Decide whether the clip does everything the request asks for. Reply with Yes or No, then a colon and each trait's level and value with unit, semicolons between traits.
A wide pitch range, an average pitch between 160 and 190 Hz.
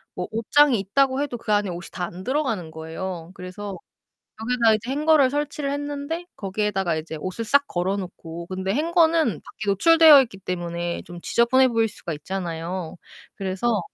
No: wide, 7.3 semitones; high, 205 Hz